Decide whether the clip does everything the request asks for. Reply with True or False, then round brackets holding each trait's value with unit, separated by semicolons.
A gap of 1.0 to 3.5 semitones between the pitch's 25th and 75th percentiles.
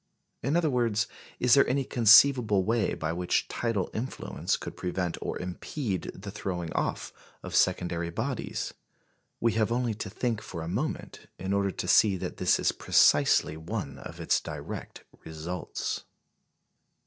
False (4.8 semitones)